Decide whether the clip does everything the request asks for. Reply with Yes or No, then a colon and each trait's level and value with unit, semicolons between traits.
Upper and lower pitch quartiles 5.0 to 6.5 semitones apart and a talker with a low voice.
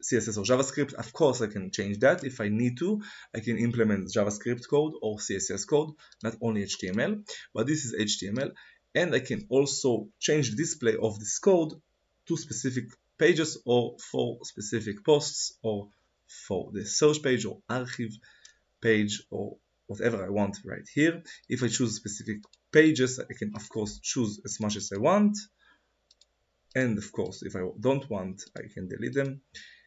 Yes: wide, 5.5 semitones; low, 120 Hz